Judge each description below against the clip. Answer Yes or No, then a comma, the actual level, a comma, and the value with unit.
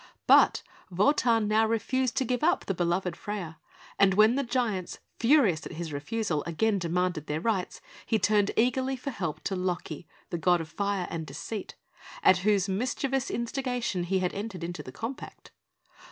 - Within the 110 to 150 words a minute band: No, average, 170 wpm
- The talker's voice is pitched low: No, high, 200 Hz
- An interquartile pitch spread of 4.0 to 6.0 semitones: Yes, average, 4.9 semitones